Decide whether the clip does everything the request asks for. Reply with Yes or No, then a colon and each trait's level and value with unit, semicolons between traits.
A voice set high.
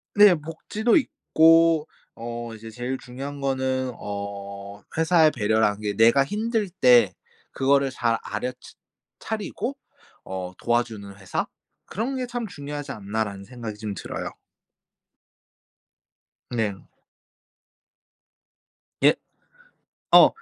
No: low, 125 Hz